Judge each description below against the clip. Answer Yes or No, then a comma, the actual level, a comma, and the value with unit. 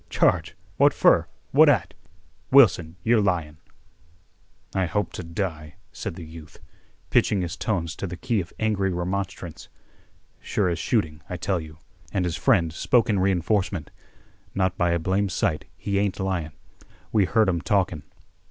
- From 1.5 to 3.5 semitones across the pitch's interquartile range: Yes, average, 3.2 semitones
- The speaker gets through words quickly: No, average, 160 wpm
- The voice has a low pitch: Yes, very low, 90 Hz